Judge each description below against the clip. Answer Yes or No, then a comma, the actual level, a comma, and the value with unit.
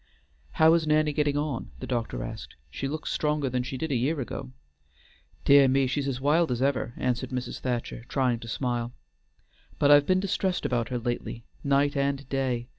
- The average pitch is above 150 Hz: No, low, 135 Hz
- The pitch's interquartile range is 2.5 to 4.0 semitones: Yes, average, 2.9 semitones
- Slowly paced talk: No, average, 185 wpm